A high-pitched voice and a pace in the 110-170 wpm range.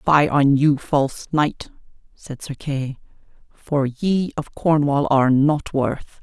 No: medium, 145 Hz; average, 145 wpm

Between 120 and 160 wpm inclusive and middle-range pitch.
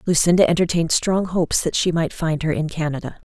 No: average, 200 wpm; medium, 165 Hz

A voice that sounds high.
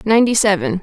Yes: high, 200 Hz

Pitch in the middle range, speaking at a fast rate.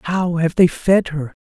Yes: medium, 170 Hz; fast, 210 wpm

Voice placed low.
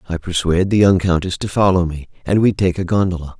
Yes: very low, 90 Hz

